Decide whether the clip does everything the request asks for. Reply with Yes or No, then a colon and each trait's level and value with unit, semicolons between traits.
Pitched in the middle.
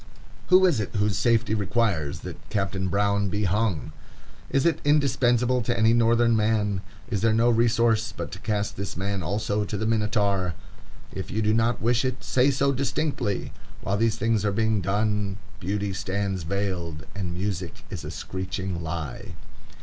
No: low, 105 Hz